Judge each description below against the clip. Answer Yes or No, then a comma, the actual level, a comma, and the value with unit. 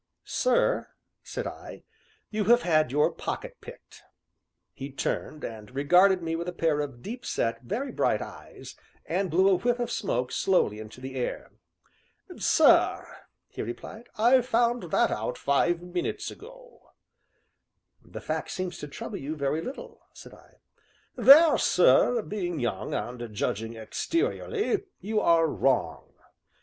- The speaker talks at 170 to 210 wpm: No, average, 140 wpm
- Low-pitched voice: No, medium, 175 Hz